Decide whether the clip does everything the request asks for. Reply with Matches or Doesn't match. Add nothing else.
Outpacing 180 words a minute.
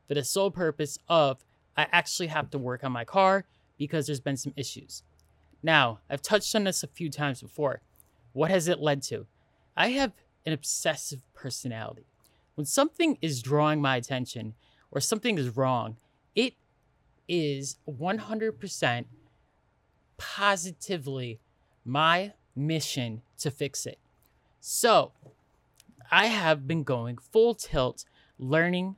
Doesn't match